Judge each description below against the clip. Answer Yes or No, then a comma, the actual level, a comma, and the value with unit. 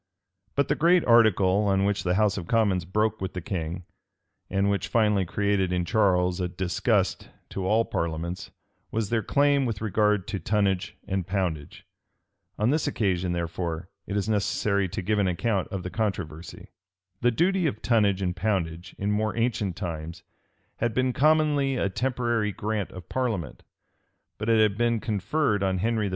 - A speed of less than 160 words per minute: No, average, 170 wpm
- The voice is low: Yes, low, 100 Hz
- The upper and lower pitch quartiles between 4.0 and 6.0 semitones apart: No, average, 3.5 semitones